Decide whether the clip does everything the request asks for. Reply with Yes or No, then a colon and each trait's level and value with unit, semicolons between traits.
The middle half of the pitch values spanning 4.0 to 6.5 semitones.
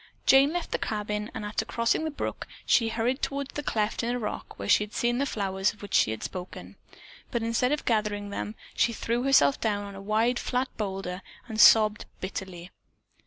No: average, 3.1 semitones